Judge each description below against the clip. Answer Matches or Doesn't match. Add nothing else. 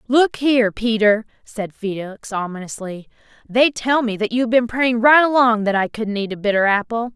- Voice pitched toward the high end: Matches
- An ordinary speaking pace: Matches